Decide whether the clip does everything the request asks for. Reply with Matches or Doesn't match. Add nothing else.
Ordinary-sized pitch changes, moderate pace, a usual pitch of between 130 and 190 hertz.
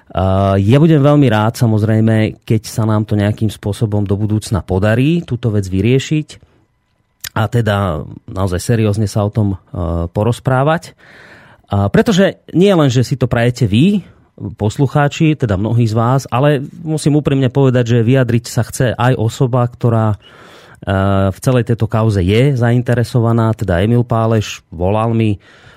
Doesn't match